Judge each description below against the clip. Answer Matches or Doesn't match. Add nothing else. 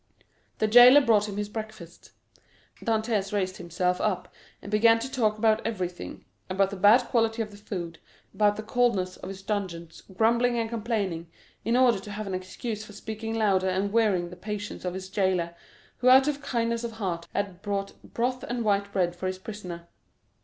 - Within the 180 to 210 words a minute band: Matches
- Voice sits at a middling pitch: Doesn't match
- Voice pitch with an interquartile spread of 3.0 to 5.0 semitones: Matches